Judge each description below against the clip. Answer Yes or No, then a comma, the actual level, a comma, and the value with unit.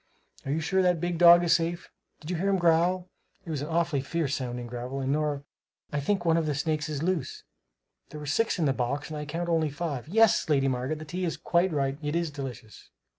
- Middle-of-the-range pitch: Yes, medium, 155 Hz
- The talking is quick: Yes, fast, 240 wpm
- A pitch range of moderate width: Yes, average, 3.5 semitones